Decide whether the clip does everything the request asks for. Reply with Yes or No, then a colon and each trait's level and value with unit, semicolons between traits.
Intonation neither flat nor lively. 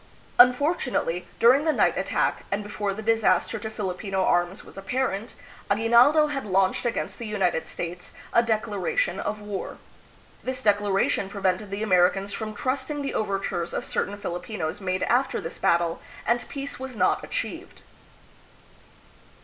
Yes: average, 4.2 semitones